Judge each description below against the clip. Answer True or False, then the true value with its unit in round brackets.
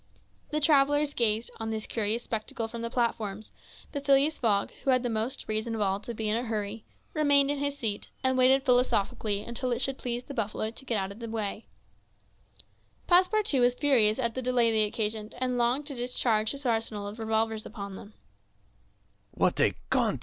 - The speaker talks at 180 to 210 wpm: True (185 wpm)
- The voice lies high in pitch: True (235 Hz)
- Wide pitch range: False (3.3 semitones)